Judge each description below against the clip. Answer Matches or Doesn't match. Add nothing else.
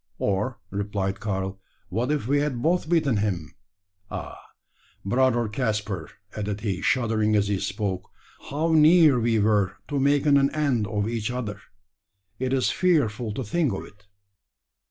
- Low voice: Matches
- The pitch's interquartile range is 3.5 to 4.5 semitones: Doesn't match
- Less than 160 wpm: Matches